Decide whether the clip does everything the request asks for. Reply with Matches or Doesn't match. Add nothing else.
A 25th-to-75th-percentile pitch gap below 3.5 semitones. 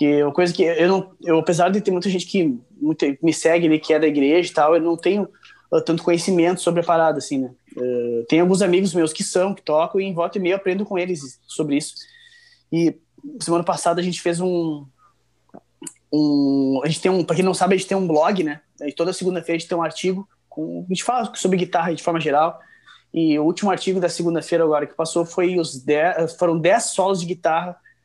Matches